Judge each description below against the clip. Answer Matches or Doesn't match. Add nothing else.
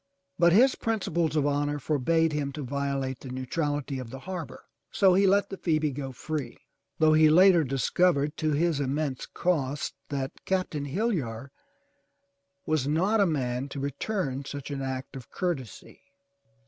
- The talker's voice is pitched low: Doesn't match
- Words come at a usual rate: Matches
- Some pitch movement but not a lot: Matches